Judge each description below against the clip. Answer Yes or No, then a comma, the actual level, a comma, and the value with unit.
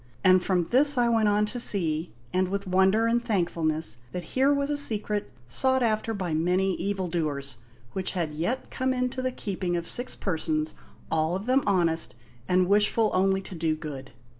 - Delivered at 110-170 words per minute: No, average, 180 wpm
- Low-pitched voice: No, high, 190 Hz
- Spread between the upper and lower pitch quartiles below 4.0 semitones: No, wide, 5.4 semitones